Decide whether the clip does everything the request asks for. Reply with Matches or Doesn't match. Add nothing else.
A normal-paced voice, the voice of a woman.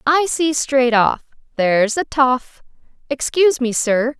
Doesn't match